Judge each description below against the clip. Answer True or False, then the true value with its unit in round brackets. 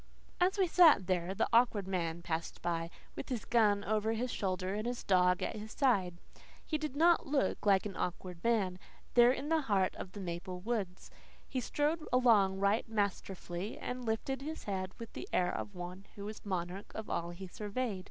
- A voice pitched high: True (205 Hz)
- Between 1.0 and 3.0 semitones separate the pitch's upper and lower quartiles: False (4.8 semitones)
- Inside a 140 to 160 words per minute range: False (190 wpm)